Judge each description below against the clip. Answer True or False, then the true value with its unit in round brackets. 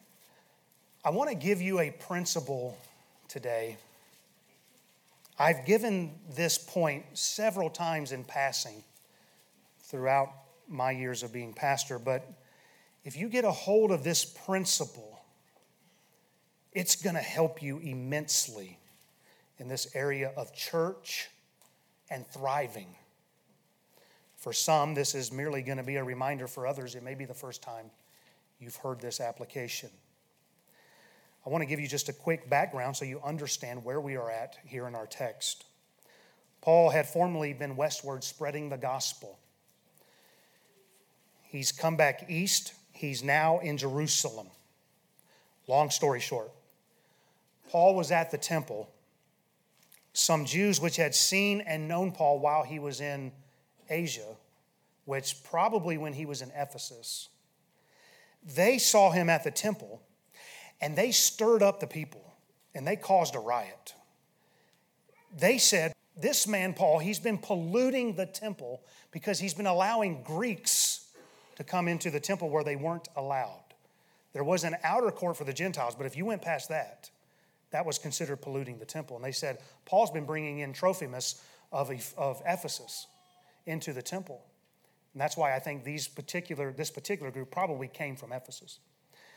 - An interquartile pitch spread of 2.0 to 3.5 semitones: False (4.3 semitones)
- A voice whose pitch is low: False (150 Hz)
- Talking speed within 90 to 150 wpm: True (145 wpm)